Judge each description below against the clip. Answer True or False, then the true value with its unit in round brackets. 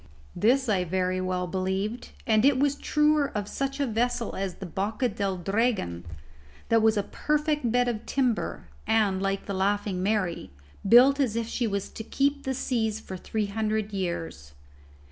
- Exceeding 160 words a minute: True (170 wpm)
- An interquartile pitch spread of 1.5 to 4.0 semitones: False (4.5 semitones)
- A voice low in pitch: False (215 Hz)